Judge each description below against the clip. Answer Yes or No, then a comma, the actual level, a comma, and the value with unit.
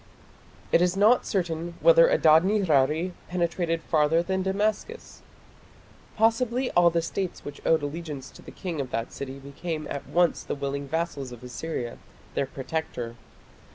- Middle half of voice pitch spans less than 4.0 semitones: No, average, 4.9 semitones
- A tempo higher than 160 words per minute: No, average, 150 wpm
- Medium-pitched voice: Yes, medium, 165 Hz